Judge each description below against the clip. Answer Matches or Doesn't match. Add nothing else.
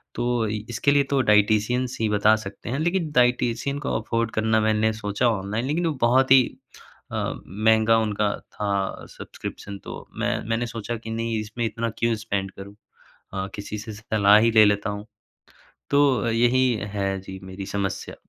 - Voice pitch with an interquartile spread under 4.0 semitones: Matches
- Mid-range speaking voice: Doesn't match